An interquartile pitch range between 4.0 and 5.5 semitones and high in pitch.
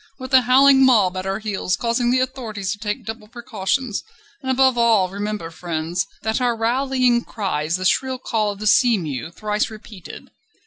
Yes: average, 4.6 semitones; high, 220 Hz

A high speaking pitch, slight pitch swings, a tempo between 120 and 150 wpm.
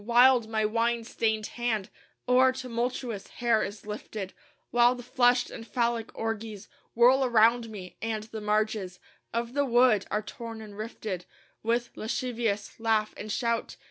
Yes: high, 225 Hz; narrow, 2.1 semitones; average, 145 wpm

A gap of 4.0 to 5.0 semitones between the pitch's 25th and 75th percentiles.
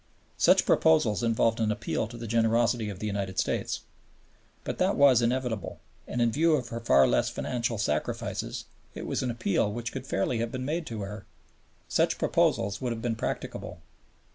No: narrow, 2.6 semitones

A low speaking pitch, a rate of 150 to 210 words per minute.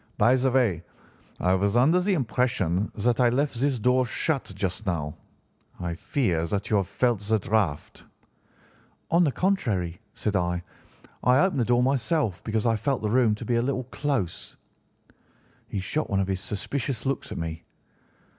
Yes: low, 115 Hz; average, 175 wpm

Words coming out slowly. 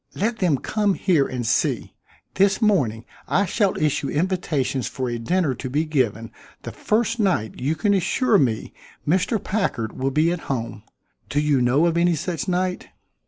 No: average, 170 wpm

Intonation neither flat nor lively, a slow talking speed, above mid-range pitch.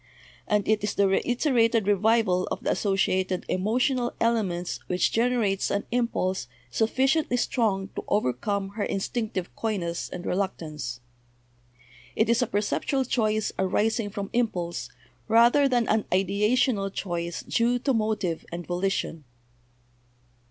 Yes: average, 3.9 semitones; slow, 125 wpm; high, 210 Hz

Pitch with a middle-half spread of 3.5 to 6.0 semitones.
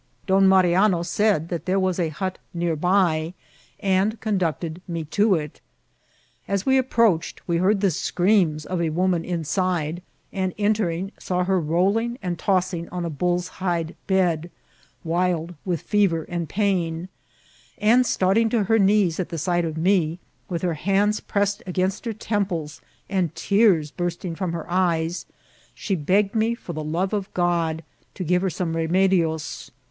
No: average, 2.8 semitones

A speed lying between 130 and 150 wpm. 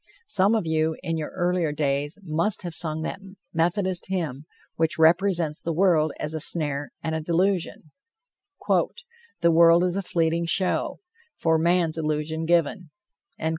Yes: average, 145 wpm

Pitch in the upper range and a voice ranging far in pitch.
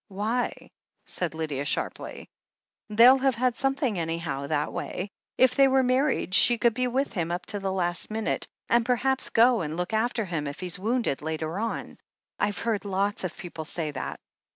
Yes: high, 205 Hz; wide, 6.4 semitones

